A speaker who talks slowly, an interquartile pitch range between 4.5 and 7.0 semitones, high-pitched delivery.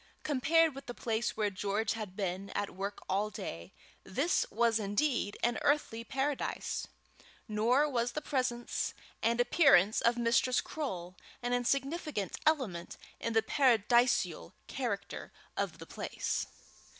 Yes: slow, 130 wpm; average, 4.8 semitones; high, 235 Hz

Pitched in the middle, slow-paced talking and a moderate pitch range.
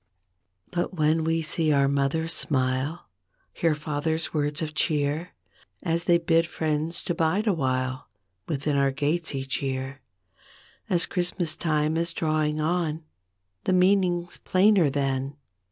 Yes: medium, 155 Hz; slow, 130 wpm; average, 3.0 semitones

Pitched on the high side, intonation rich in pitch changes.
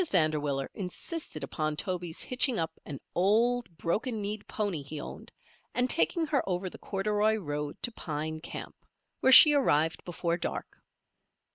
No: medium, 180 Hz; wide, 6.5 semitones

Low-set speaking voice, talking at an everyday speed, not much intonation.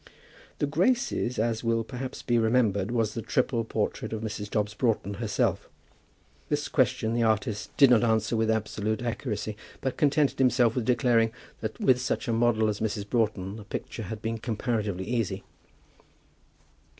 Yes: low, 115 Hz; average, 160 wpm; narrow, 2.2 semitones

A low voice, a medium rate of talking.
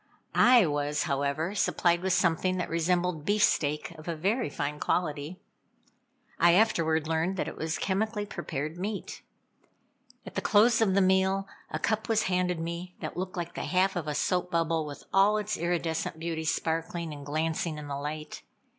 No: medium, 170 Hz; average, 170 wpm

